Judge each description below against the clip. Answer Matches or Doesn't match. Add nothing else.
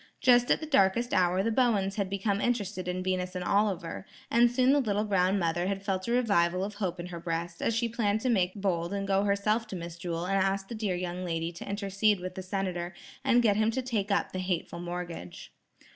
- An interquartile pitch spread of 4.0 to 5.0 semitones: Doesn't match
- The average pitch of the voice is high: Matches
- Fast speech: Matches